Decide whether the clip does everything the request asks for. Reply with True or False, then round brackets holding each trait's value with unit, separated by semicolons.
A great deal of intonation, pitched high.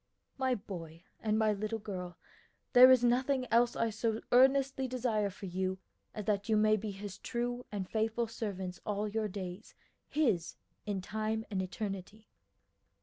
False (3.3 semitones; 215 Hz)